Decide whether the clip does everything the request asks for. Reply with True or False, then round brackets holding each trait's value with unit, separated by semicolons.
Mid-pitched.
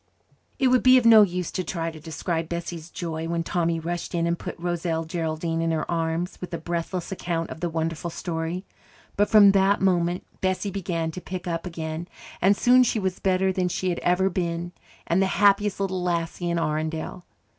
True (175 Hz)